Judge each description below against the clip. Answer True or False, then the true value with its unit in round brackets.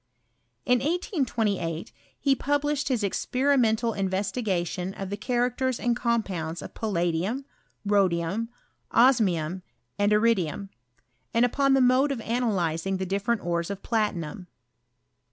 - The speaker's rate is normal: False (115 wpm)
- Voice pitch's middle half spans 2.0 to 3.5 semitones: False (5.1 semitones)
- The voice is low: False (210 Hz)